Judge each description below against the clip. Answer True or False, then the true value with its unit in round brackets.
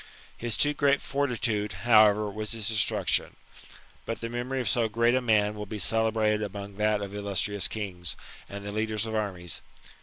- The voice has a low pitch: True (110 Hz)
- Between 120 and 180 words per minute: True (175 wpm)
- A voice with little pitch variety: True (2.1 semitones)